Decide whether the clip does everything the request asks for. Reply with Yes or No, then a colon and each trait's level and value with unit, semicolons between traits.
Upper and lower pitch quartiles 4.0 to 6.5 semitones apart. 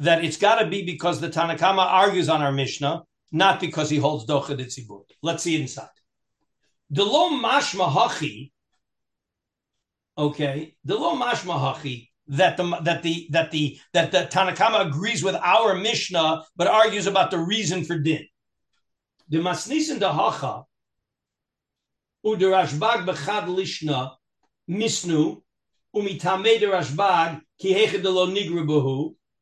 Yes: average, 4.3 semitones